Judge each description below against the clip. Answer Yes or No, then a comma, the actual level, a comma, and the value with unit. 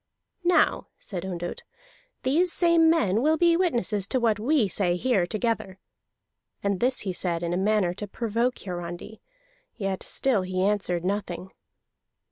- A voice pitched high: Yes, high, 205 Hz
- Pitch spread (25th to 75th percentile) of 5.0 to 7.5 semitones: Yes, wide, 5.5 semitones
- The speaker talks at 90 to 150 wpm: Yes, average, 145 wpm